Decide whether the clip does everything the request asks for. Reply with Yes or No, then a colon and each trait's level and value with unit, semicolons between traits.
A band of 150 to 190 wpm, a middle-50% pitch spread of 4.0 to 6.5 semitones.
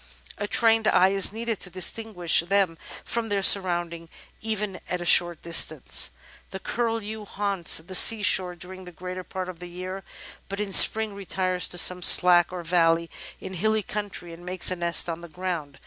No: average, 180 wpm; average, 2.7 semitones